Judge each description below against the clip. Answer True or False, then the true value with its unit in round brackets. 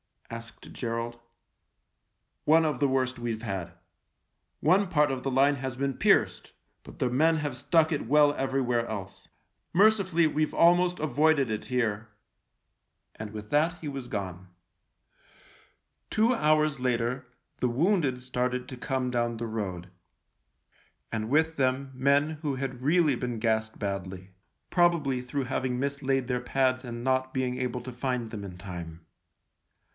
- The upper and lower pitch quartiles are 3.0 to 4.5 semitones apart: True (3.9 semitones)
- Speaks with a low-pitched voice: True (130 Hz)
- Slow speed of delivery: False (155 wpm)